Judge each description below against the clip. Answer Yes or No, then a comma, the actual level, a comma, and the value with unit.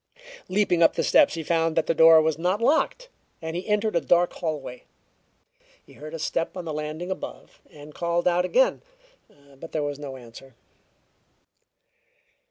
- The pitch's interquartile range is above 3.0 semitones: No, average, 2.7 semitones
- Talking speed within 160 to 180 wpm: Yes, average, 170 wpm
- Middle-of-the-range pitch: Yes, medium, 165 Hz